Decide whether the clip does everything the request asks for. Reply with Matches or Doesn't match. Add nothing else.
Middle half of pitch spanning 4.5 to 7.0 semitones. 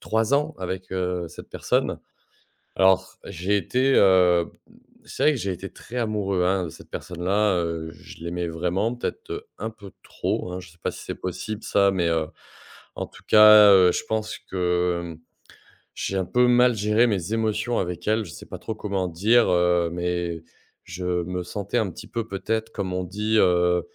Doesn't match